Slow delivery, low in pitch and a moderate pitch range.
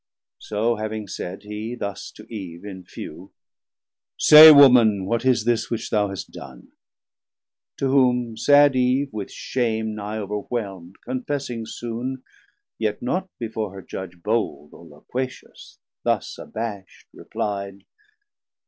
Yes: slow, 130 wpm; low, 110 Hz; average, 3.7 semitones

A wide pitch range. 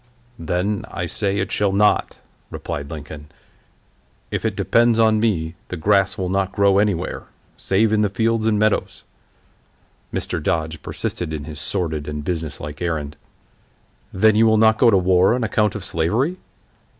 No: average, 5.0 semitones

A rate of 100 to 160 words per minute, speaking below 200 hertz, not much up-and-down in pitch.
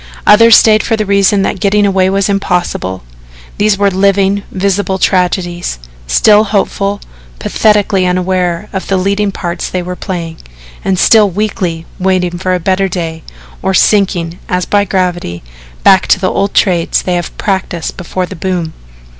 Yes: average, 155 wpm; high, 190 Hz; narrow, 2.0 semitones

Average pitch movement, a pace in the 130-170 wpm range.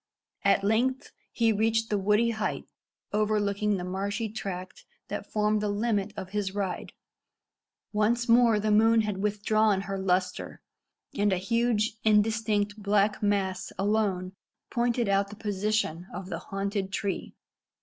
No: narrow, 1.9 semitones; average, 140 wpm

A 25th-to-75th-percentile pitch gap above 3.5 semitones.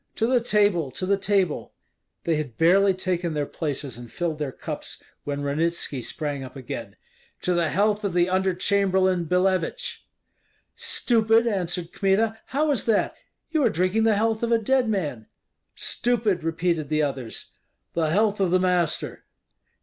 Yes: average, 5.2 semitones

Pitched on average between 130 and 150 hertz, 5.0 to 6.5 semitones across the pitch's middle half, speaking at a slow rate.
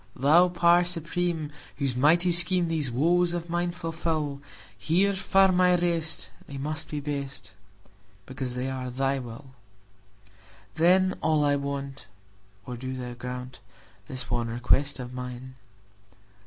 Yes: medium, 140 Hz; wide, 5.6 semitones; slow, 115 wpm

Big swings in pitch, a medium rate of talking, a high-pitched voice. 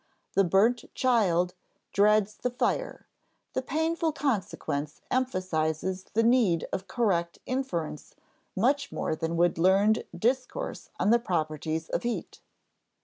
No: wide, 6.5 semitones; slow, 120 wpm; high, 200 Hz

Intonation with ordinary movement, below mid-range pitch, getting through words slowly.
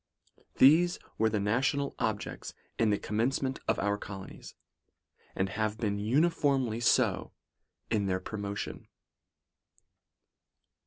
Yes: average, 4.6 semitones; low, 110 Hz; slow, 120 wpm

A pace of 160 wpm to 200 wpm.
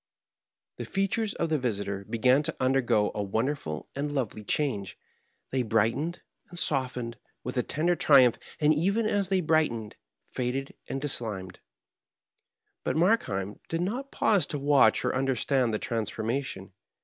No: average, 145 wpm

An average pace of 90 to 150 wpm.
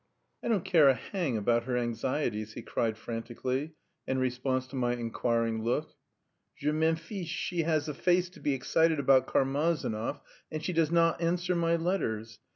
No: average, 170 wpm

